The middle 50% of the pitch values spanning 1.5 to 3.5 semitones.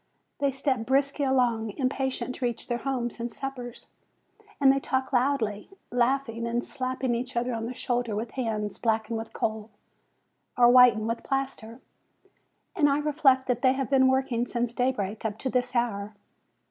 Yes: narrow, 2.5 semitones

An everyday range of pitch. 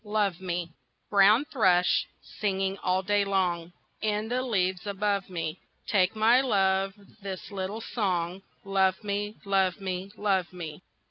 No: narrow, 2.2 semitones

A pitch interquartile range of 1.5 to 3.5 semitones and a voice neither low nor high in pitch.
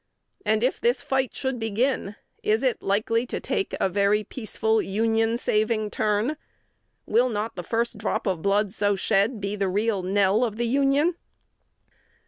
No: average, 2.8 semitones; high, 220 Hz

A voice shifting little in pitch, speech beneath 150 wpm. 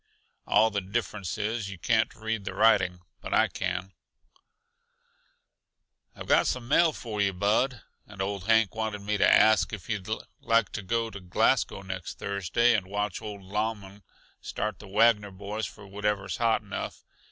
No: narrow, 2.3 semitones; average, 165 wpm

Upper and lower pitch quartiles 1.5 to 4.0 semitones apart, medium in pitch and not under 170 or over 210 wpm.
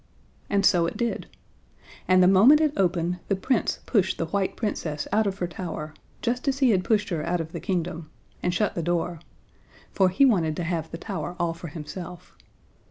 Yes: average, 3.3 semitones; medium, 180 Hz; average, 200 wpm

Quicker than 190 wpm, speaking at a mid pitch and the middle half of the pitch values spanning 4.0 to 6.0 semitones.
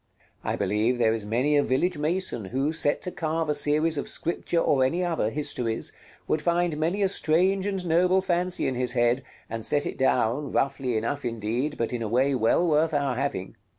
Yes: average, 200 wpm; medium, 145 Hz; wide, 5.4 semitones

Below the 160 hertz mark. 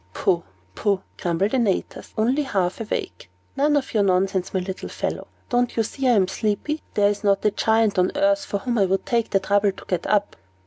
No: high, 205 Hz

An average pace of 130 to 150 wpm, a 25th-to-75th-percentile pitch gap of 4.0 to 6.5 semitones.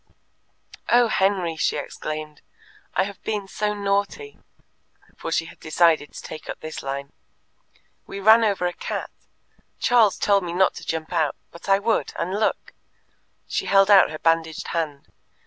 No: average, 160 wpm; average, 4.3 semitones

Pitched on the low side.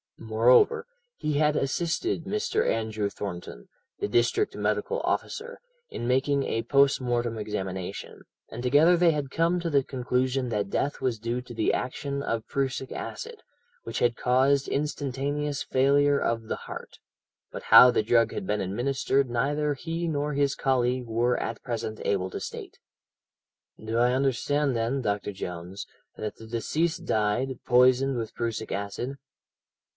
Yes: low, 125 Hz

